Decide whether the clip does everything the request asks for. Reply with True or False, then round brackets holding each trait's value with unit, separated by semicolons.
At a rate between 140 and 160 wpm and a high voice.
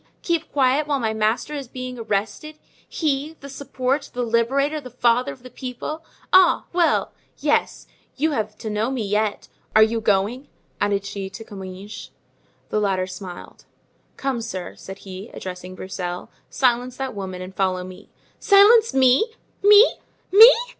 True (155 wpm; 235 Hz)